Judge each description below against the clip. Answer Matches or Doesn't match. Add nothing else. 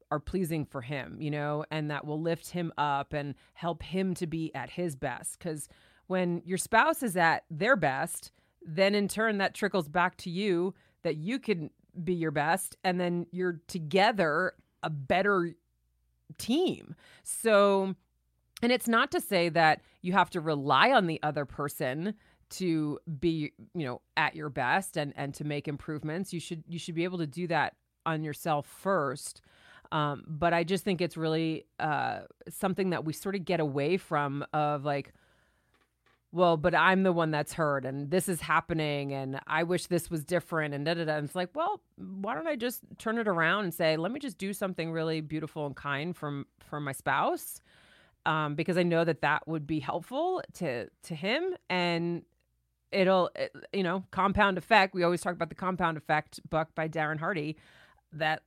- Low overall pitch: Doesn't match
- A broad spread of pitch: Doesn't match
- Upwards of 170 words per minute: Matches